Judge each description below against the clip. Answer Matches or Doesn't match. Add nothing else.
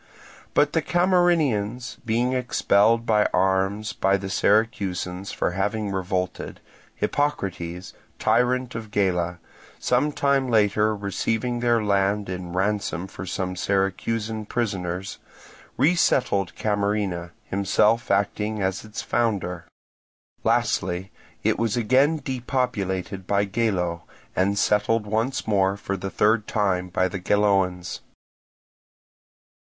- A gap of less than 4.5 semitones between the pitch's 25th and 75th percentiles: Matches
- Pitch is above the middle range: Doesn't match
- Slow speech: Matches